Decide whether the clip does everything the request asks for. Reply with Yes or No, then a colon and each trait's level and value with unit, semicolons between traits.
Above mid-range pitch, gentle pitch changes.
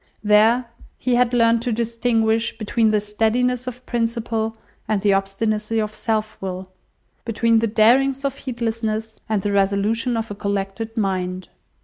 Yes: high, 225 Hz; narrow, 1.9 semitones